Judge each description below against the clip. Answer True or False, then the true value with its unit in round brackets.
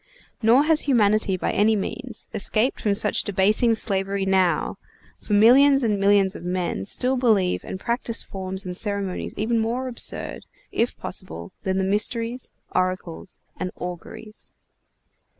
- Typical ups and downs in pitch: True (3.4 semitones)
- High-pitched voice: True (205 Hz)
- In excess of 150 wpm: False (140 wpm)